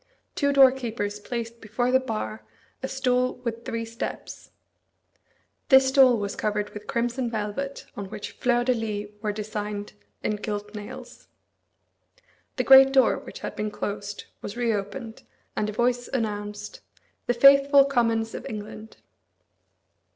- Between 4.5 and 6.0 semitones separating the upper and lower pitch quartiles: No, average, 3.4 semitones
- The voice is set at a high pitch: Yes, high, 225 Hz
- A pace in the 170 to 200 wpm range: No, slow, 135 wpm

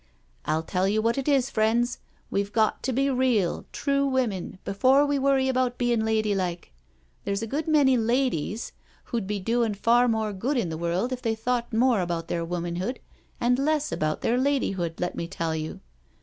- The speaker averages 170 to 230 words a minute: Yes, average, 185 wpm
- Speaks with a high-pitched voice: Yes, high, 230 Hz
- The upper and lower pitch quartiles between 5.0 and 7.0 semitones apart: Yes, wide, 5.5 semitones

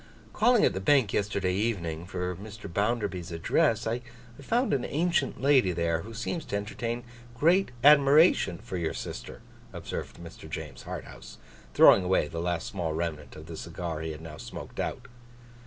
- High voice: No, very low, 95 Hz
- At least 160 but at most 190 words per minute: Yes, average, 165 wpm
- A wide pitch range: Yes, wide, 7.0 semitones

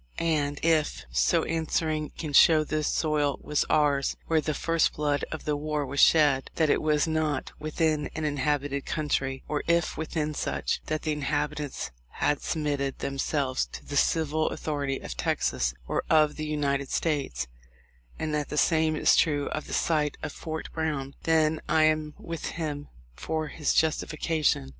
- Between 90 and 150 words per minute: No, average, 165 wpm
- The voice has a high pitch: No, medium, 150 Hz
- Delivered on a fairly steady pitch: Yes, narrow, 1.6 semitones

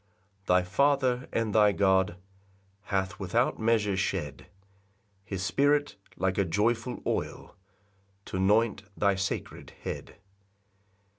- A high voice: No, low, 105 Hz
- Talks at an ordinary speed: No, slow, 105 wpm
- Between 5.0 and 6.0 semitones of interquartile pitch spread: No, average, 3.6 semitones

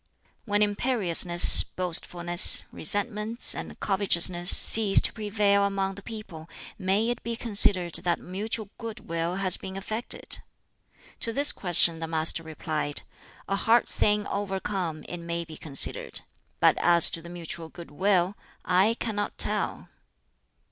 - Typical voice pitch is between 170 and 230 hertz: Yes, high, 190 Hz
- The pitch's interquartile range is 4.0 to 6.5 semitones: No, average, 3.5 semitones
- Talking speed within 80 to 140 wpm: Yes, slow, 135 wpm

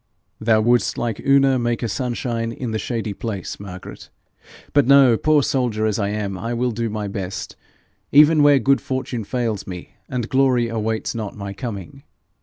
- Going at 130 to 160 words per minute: No, average, 175 wpm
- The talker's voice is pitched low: Yes, low, 115 Hz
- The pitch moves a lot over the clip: No, average, 3.4 semitones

